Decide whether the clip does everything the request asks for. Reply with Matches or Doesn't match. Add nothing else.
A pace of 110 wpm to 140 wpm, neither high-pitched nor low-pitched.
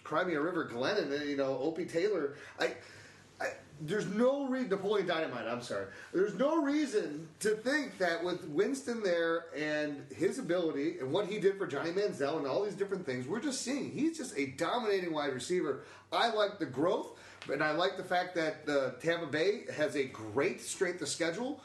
Doesn't match